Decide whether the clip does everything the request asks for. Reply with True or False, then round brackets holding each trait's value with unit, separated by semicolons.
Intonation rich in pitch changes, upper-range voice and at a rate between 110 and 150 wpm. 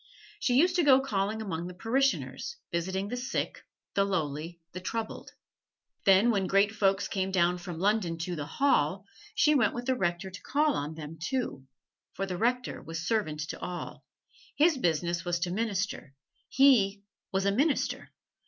False (5.8 semitones; 195 Hz; 170 wpm)